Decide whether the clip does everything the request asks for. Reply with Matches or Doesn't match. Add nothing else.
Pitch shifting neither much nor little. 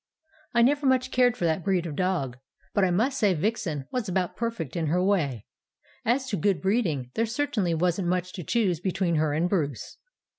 Doesn't match